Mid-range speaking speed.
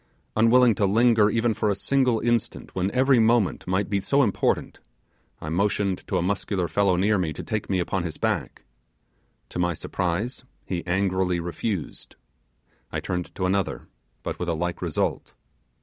Yes: average, 165 wpm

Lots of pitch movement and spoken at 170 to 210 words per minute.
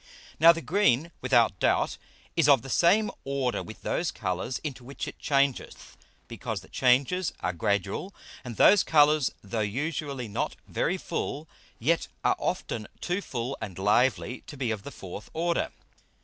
No: wide, 6.2 semitones; average, 160 wpm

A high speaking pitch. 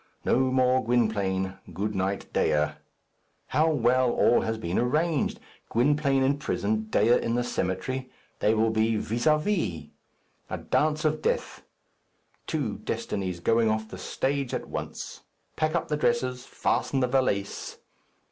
No: low, 120 Hz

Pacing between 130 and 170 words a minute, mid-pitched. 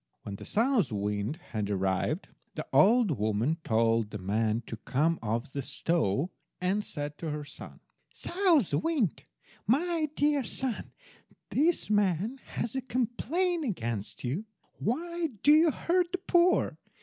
Yes: average, 140 wpm; medium, 180 Hz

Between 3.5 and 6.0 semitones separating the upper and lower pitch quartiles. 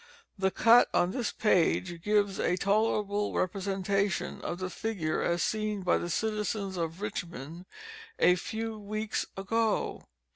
No: average, 3.0 semitones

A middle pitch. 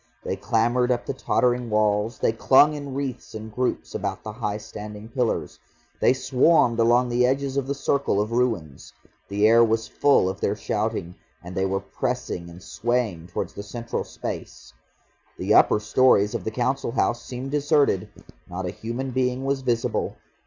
No: low, 115 Hz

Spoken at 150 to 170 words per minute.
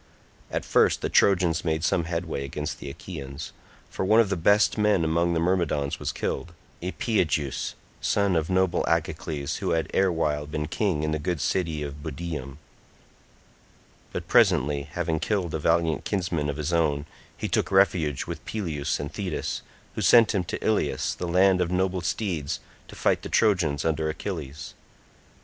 Yes: average, 165 wpm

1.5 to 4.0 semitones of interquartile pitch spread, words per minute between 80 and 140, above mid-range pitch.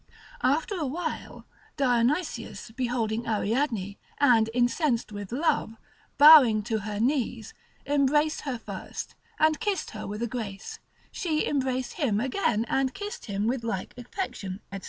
No: average, 4.9 semitones; slow, 135 wpm; high, 245 Hz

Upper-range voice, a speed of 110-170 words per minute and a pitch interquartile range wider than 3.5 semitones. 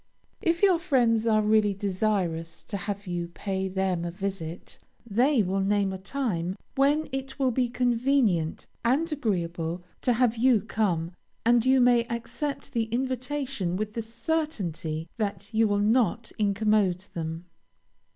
Yes: high, 215 Hz; average, 145 wpm; average, 5.0 semitones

